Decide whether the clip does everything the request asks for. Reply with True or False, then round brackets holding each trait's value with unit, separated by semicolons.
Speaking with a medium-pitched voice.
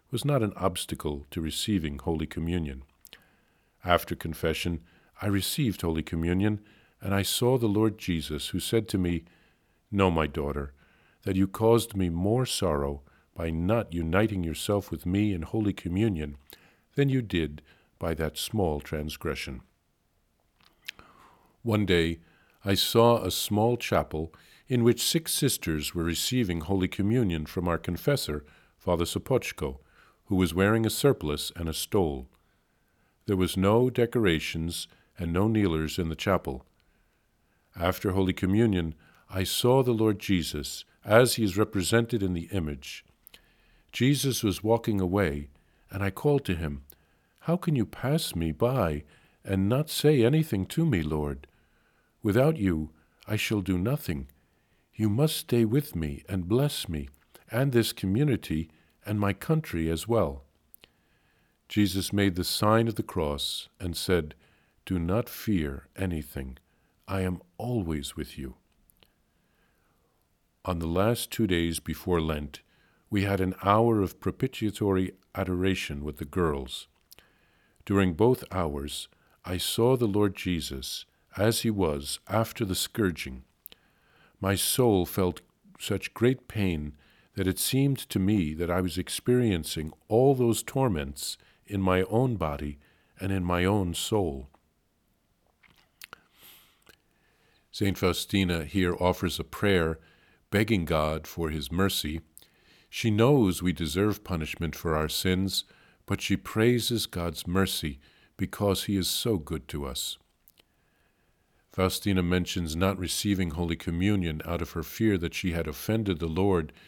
False (95 Hz)